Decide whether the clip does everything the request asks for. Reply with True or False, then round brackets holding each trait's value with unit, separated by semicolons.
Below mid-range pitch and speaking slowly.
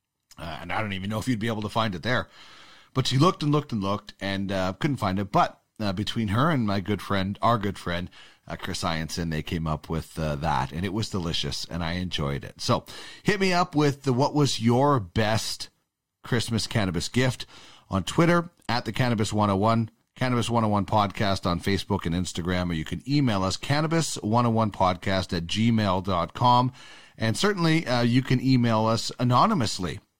False (110 Hz; 190 wpm)